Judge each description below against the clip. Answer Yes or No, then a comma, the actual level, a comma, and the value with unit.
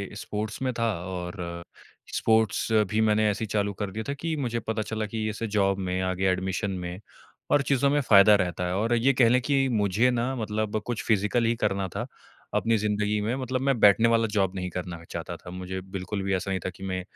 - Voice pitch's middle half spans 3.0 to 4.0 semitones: Yes, average, 3.4 semitones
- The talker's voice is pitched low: Yes, low, 105 Hz